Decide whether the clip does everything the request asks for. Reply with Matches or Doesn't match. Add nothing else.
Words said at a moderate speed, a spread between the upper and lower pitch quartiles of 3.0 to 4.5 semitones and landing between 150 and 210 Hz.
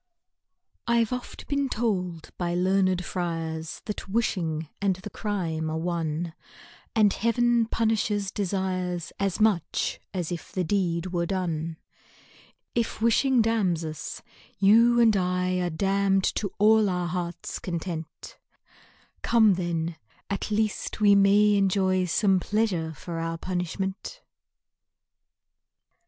Doesn't match